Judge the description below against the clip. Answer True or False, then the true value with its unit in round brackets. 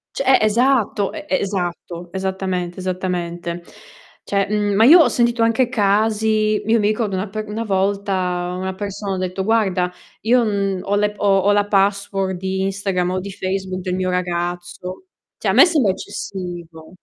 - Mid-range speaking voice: False (195 Hz)